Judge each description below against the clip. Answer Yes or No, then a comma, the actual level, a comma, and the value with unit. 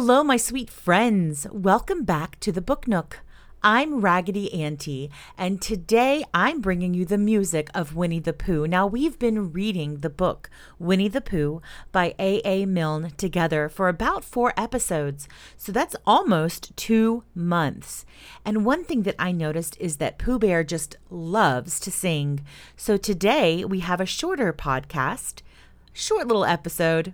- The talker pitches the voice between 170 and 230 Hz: Yes, medium, 185 Hz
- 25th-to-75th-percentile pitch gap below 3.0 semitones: No, average, 4.7 semitones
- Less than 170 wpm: Yes, average, 155 wpm